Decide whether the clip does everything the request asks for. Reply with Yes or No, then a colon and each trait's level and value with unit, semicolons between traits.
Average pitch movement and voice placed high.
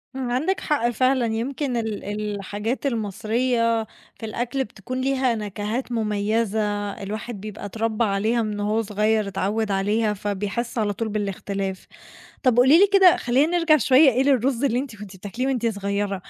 Yes: average, 3.7 semitones; high, 225 Hz